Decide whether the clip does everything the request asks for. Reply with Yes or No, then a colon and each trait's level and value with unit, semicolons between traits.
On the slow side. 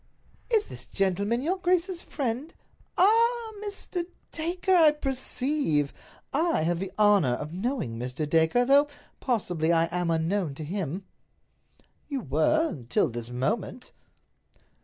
Yes: slow, 115 wpm